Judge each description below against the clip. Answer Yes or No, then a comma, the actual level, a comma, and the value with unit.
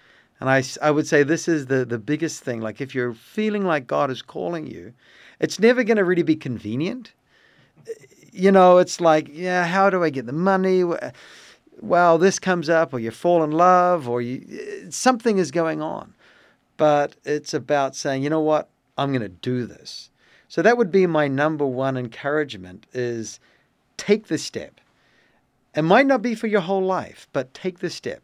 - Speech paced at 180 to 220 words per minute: Yes, average, 190 wpm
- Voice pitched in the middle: Yes, medium, 160 Hz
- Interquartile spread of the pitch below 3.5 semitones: No, wide, 5.4 semitones